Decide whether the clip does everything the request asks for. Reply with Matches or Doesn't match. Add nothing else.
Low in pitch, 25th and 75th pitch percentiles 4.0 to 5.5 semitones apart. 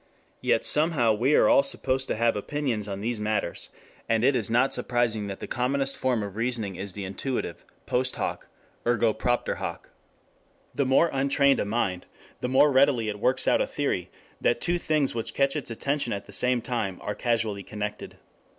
Matches